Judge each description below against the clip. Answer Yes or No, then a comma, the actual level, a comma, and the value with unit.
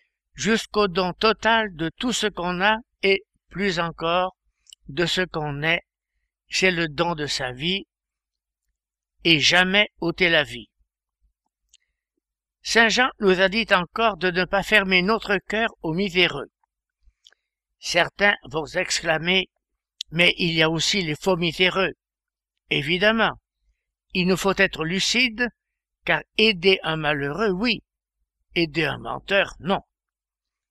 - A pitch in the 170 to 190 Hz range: Yes, medium, 185 Hz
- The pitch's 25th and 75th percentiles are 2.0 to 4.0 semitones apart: No, average, 4.4 semitones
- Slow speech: Yes, slow, 130 wpm